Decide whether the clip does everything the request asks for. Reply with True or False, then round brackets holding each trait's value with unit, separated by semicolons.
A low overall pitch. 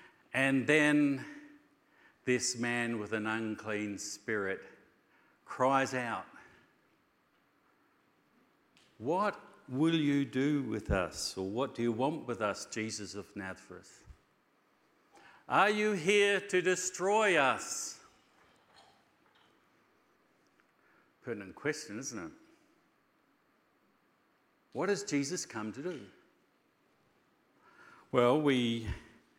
True (130 Hz)